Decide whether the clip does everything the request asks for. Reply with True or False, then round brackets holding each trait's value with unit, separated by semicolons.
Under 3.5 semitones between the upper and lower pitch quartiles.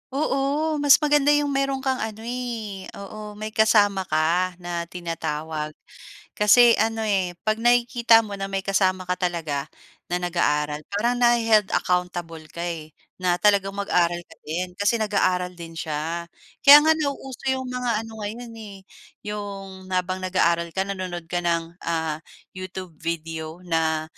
False (4.7 semitones)